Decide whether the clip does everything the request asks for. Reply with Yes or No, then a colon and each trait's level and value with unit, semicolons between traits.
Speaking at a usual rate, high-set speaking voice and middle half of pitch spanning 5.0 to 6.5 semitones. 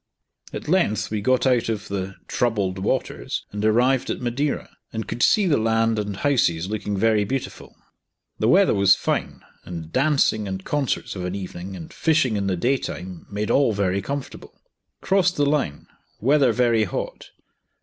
No: average, 170 wpm; low, 110 Hz; wide, 5.4 semitones